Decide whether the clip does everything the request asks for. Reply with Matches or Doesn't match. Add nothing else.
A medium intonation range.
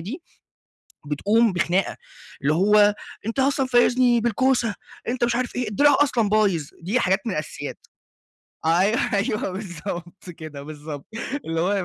Doesn't match